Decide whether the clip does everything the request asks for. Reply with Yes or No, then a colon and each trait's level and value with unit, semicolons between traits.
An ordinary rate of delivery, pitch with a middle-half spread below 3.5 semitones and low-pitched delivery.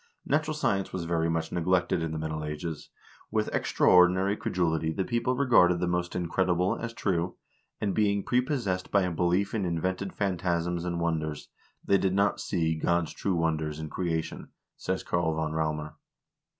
Yes: average, 165 wpm; average, 3.1 semitones; very low, 90 Hz